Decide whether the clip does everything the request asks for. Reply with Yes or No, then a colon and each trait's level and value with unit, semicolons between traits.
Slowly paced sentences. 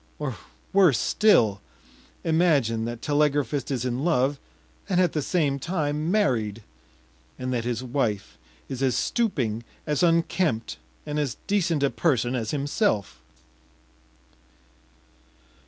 Yes: slow, 120 wpm